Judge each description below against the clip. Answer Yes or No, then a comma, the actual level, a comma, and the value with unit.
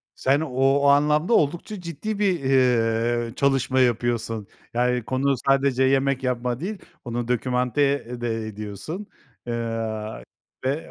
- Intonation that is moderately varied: Yes, average, 3.1 semitones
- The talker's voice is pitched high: No, low, 130 Hz